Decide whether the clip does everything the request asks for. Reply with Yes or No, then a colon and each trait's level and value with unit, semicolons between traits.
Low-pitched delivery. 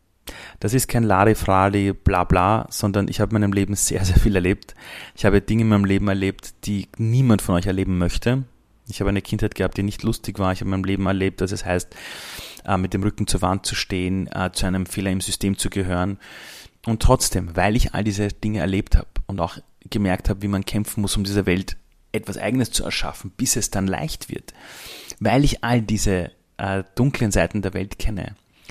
Yes: low, 100 Hz